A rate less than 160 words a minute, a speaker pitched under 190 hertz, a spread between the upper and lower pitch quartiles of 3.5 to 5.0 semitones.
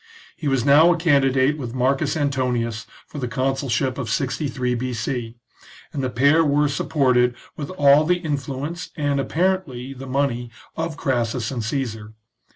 No: average, 150 wpm; low, 135 Hz; average, 2.8 semitones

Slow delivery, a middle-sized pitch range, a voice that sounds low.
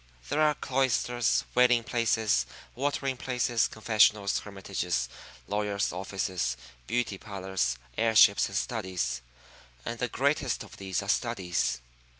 Yes: slow, 120 wpm; average, 4.3 semitones; low, 110 Hz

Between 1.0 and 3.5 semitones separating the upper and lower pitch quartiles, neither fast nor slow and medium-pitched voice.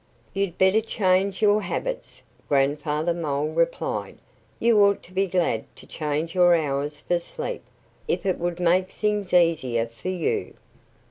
No: average, 4.2 semitones; average, 145 wpm; medium, 175 Hz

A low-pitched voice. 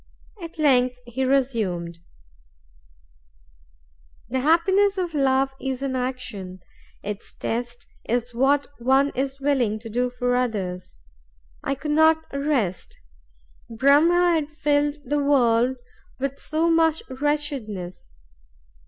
No: very high, 265 Hz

